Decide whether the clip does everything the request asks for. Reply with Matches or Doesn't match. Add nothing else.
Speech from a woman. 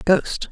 Doesn't match